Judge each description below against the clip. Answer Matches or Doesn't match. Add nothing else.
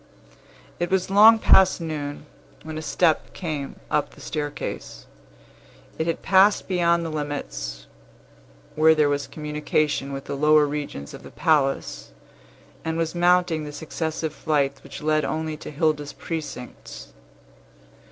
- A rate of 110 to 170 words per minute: Matches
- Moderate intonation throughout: Doesn't match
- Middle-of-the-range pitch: Matches